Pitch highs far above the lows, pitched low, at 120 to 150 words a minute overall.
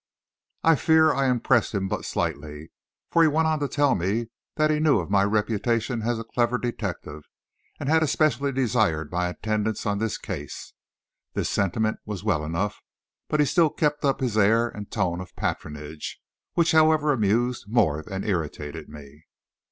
No: wide, 7.2 semitones; low, 110 Hz; average, 170 wpm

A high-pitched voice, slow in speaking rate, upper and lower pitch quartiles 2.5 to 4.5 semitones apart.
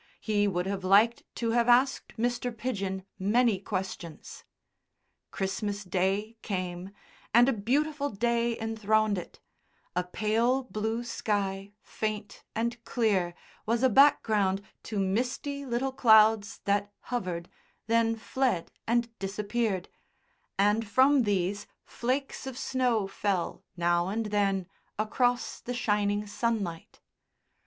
Yes: high, 215 Hz; slow, 115 wpm; average, 3.4 semitones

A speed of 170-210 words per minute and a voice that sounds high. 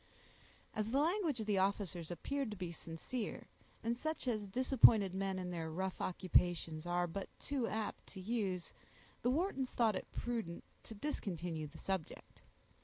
No: average, 160 wpm; high, 200 Hz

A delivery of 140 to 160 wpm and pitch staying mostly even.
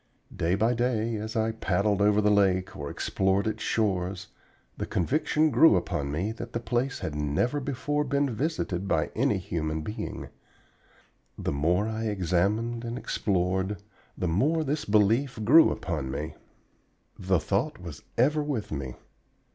No: average, 150 wpm; average, 5.1 semitones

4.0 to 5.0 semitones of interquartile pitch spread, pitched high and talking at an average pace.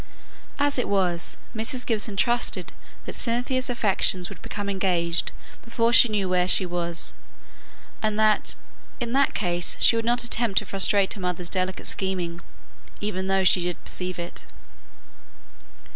Yes: average, 4.3 semitones; high, 195 Hz; average, 145 wpm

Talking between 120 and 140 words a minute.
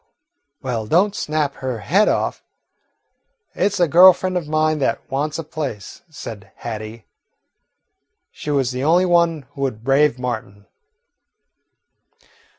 Yes: slow, 135 wpm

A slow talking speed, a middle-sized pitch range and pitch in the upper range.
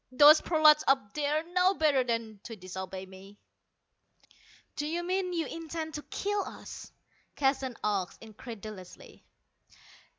No: slow, 125 wpm; wide, 7.1 semitones; very high, 270 Hz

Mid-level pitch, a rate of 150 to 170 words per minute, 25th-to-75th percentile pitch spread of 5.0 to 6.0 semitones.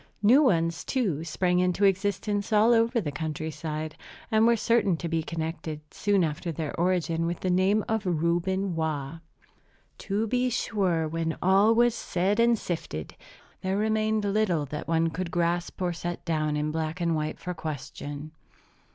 No: medium, 175 Hz; average, 165 wpm; average, 4.3 semitones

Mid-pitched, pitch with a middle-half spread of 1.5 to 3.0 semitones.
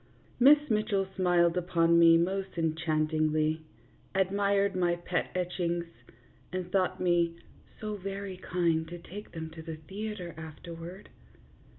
Yes: medium, 175 Hz; average, 2.7 semitones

